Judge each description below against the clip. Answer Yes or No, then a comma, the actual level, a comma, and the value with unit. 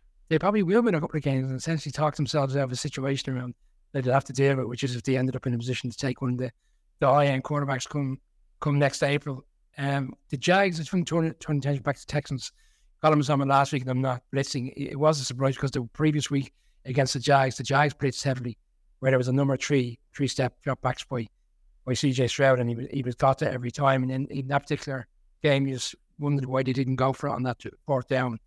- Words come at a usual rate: No, fast, 255 wpm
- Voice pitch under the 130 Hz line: No, low, 135 Hz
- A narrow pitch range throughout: Yes, narrow, 2.0 semitones